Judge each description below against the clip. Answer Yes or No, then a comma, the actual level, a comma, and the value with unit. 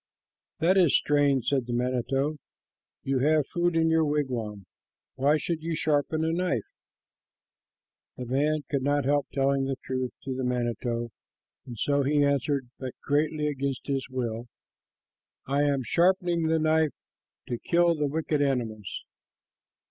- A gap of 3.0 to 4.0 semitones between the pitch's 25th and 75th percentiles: Yes, average, 3.3 semitones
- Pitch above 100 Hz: Yes, medium, 140 Hz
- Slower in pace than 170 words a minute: Yes, average, 145 wpm